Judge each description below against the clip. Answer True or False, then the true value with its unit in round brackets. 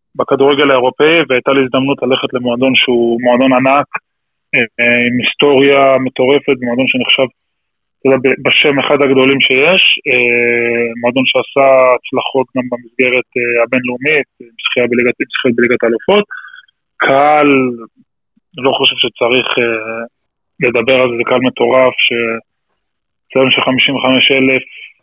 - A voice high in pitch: False (130 Hz)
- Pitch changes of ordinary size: False (2.0 semitones)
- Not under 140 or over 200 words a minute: False (105 wpm)